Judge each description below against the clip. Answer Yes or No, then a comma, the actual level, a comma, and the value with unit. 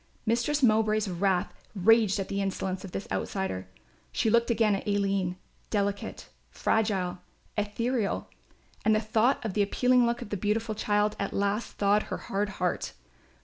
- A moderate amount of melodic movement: No, narrow, 2.1 semitones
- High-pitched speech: Yes, high, 205 Hz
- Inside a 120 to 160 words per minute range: Yes, average, 155 wpm